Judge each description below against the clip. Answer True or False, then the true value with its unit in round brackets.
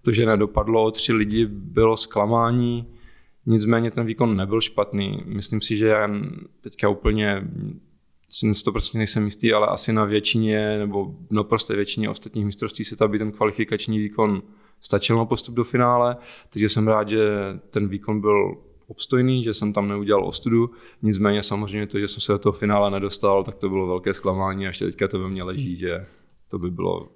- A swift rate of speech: True (180 wpm)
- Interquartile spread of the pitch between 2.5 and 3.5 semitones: False (2.0 semitones)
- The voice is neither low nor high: False (105 Hz)